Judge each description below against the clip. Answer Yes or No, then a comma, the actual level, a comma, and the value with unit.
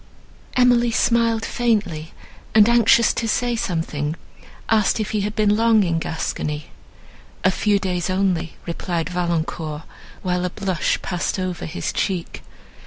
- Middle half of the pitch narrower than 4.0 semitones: No, average, 4.8 semitones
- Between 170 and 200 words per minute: No, slow, 135 wpm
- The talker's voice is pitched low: No, high, 190 Hz